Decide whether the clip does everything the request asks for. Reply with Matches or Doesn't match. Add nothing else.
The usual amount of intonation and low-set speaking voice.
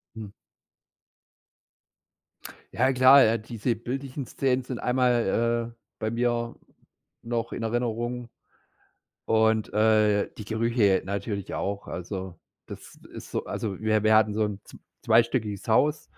Doesn't match